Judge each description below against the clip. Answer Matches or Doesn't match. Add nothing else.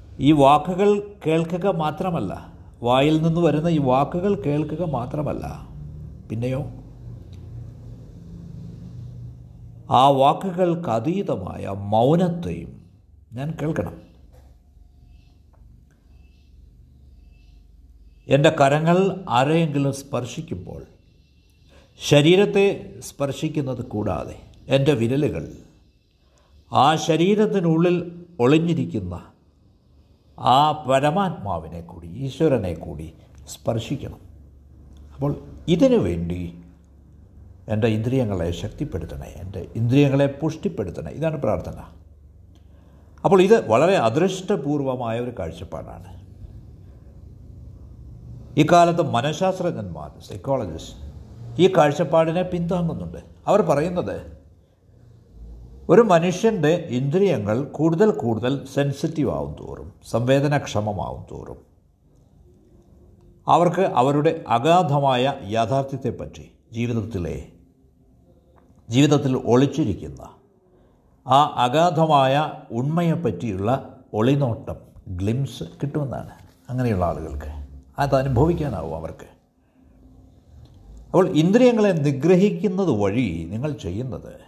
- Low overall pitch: Matches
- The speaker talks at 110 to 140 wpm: Doesn't match